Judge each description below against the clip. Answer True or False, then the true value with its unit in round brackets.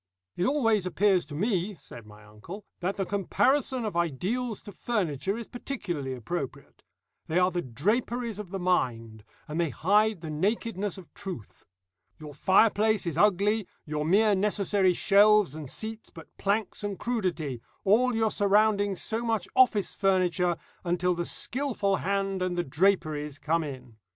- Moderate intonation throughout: True (4.6 semitones)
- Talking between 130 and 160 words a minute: True (155 wpm)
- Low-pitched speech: False (190 Hz)